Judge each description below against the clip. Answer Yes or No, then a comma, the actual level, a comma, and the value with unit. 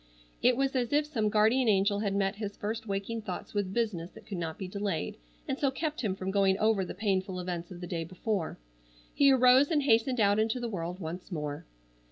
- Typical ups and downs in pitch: Yes, average, 4.0 semitones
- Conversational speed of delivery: No, fast, 220 wpm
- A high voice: Yes, high, 205 Hz